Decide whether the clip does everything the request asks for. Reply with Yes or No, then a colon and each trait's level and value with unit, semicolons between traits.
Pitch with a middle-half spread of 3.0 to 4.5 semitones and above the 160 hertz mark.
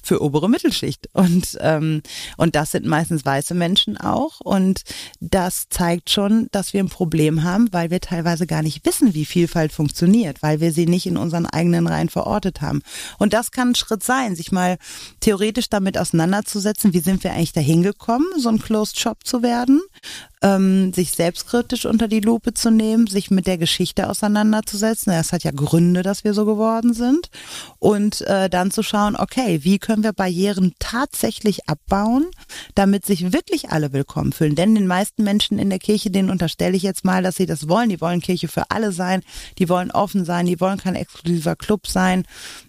Yes: average, 4.0 semitones; high, 190 Hz